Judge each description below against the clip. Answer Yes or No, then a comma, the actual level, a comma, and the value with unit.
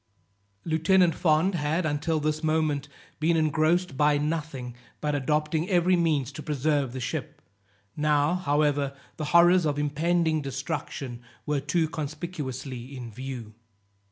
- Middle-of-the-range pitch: Yes, medium, 150 Hz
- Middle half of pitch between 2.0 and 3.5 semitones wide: Yes, narrow, 2.5 semitones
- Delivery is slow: Yes, slow, 130 wpm